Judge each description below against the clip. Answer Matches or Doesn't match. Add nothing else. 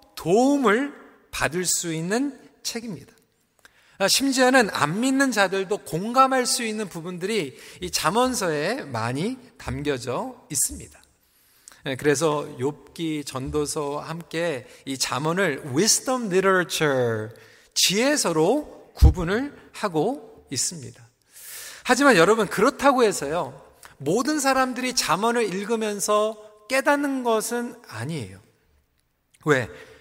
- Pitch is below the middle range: Doesn't match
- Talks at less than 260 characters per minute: Matches